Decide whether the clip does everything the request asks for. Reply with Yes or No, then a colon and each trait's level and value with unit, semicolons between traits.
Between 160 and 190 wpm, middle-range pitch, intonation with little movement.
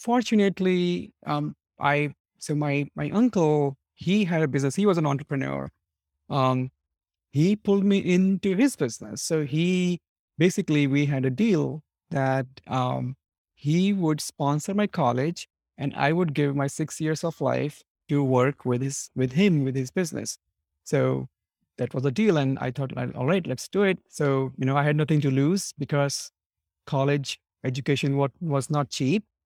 No: average, 165 wpm; medium, 145 Hz; average, 4.8 semitones